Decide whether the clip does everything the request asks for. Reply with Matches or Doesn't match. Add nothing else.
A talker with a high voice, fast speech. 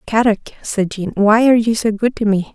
Matches